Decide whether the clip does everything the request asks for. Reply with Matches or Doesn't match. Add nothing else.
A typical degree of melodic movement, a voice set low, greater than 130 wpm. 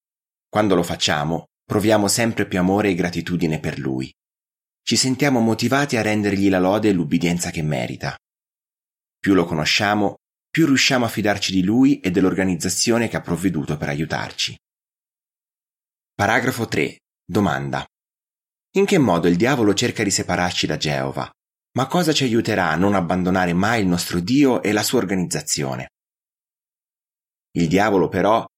Matches